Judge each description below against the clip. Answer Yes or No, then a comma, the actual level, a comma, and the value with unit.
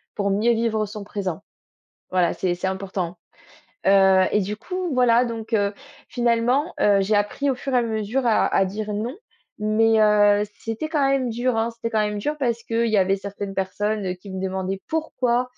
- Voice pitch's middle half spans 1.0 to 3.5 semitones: Yes, average, 3.2 semitones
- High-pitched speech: Yes, high, 215 Hz